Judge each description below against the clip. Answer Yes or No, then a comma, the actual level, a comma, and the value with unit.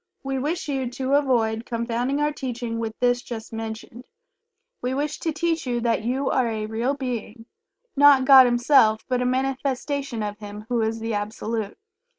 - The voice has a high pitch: Yes, high, 245 Hz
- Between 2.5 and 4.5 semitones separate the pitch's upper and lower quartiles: Yes, average, 3.1 semitones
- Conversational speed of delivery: Yes, average, 170 wpm